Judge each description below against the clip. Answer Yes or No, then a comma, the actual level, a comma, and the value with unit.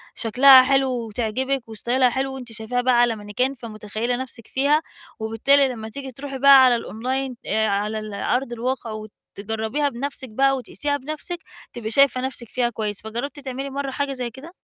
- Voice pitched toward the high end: Yes, very high, 250 Hz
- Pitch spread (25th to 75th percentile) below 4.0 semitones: Yes, average, 3.5 semitones